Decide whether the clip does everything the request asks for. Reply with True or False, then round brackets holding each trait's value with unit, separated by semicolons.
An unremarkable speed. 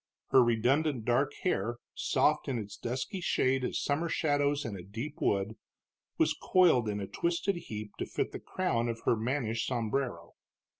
True (165 wpm)